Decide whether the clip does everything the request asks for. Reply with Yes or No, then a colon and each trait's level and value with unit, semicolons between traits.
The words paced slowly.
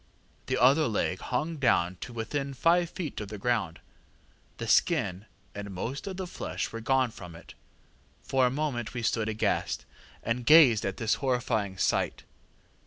No: average, 165 wpm